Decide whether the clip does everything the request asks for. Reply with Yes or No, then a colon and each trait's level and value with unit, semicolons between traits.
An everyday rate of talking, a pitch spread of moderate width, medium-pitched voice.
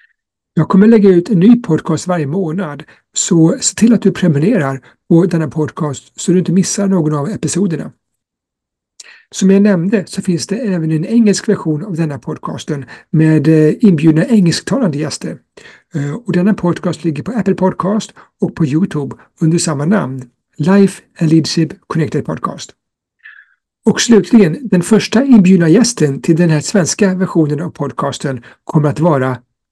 Yes: average, 155 wpm; average, 4.3 semitones; medium, 175 Hz